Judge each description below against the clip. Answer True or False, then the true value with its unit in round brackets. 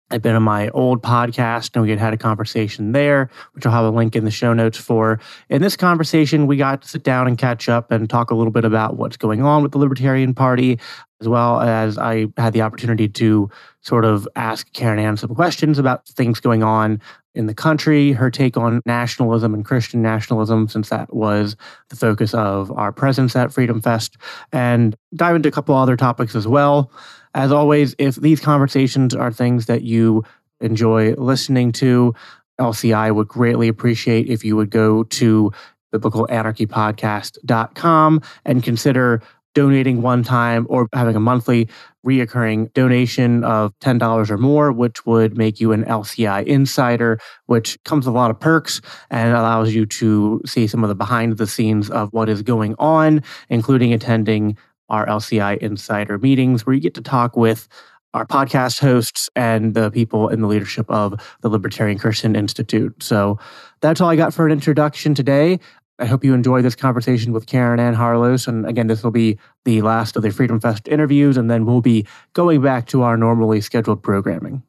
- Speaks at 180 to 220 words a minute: True (185 wpm)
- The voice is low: True (120 Hz)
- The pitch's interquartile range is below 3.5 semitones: True (2.9 semitones)